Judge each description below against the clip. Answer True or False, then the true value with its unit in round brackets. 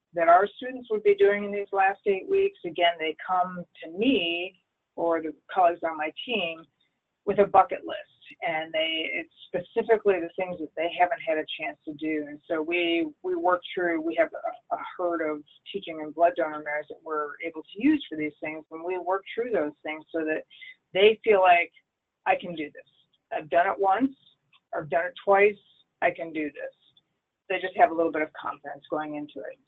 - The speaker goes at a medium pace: False (210 wpm)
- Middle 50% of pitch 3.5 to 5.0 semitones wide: True (4.5 semitones)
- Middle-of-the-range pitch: True (175 Hz)